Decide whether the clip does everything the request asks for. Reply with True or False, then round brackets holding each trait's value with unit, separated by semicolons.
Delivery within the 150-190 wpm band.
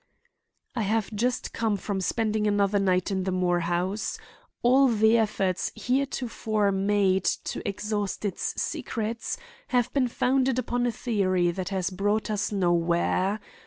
False (140 wpm)